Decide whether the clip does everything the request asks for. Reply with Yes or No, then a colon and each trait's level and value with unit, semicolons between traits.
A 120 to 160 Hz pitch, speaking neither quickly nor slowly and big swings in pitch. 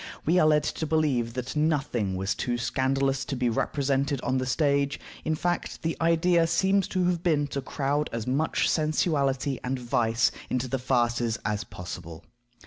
No: low, 135 Hz; average, 170 wpm; average, 4.1 semitones